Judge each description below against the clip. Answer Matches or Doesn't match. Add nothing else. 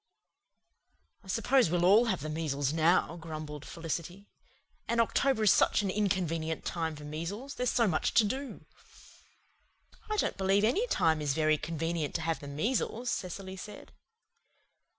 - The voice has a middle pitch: Matches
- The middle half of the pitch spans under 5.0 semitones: Doesn't match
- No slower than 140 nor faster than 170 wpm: Matches